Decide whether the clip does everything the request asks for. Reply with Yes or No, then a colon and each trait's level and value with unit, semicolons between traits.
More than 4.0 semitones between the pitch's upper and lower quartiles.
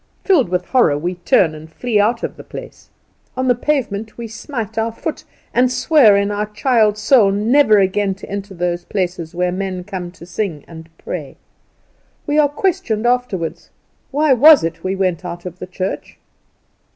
Yes: wide, 5.5 semitones